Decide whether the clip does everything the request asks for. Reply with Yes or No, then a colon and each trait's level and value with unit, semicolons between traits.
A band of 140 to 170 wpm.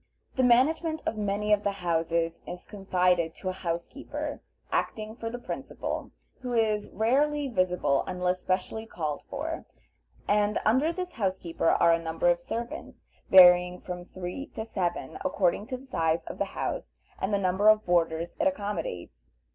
Yes: average, 160 wpm